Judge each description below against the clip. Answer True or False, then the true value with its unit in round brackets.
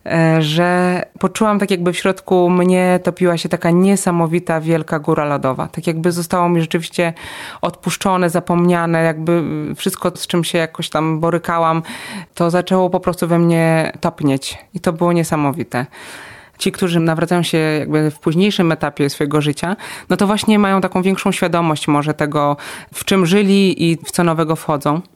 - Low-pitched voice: False (170 Hz)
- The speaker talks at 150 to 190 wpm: True (160 wpm)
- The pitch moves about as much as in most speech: False (2.1 semitones)